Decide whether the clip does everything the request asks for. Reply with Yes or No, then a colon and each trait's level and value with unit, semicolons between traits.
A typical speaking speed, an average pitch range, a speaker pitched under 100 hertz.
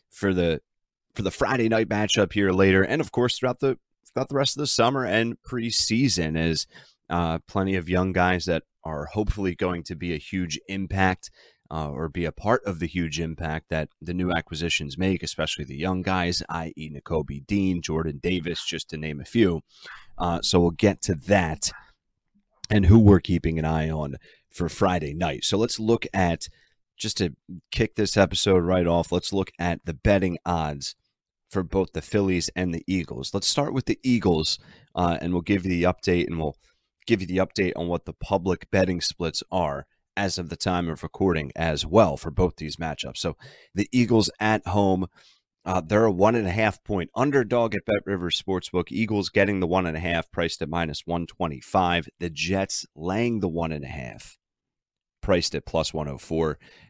Yes: average, 190 wpm; average, 3.5 semitones; very low, 90 Hz